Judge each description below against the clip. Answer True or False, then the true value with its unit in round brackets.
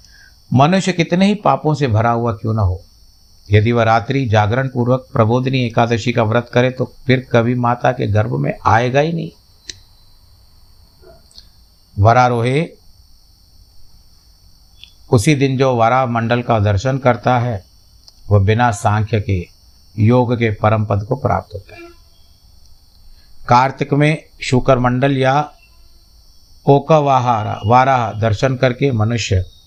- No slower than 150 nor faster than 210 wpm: False (125 wpm)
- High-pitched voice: False (115 Hz)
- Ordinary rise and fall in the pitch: False (5.8 semitones)